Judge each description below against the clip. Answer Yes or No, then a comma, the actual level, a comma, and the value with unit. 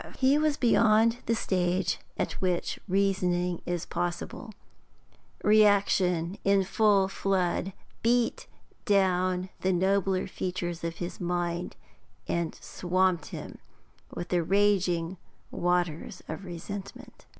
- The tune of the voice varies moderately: No, narrow, 2.2 semitones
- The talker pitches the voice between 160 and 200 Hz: Yes, medium, 185 Hz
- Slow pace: Yes, slow, 105 wpm